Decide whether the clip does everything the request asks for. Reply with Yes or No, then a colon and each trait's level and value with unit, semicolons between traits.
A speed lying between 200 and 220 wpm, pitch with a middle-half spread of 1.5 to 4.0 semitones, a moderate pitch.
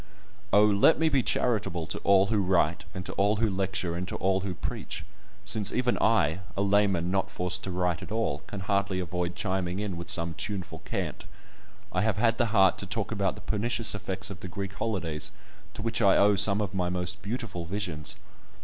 No: fast, 205 wpm; narrow, 2.6 semitones; very low, 95 Hz